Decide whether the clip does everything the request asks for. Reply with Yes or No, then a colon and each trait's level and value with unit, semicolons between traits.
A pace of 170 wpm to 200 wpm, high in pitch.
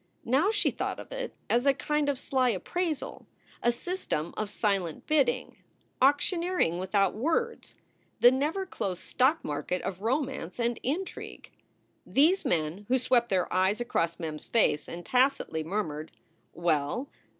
No: average, 145 wpm; high, 240 Hz